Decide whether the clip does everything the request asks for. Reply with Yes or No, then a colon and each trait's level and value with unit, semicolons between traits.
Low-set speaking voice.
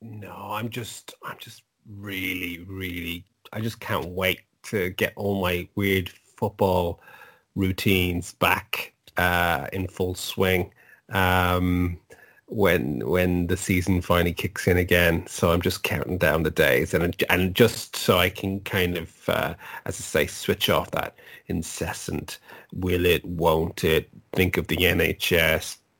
Yes: very low, 95 Hz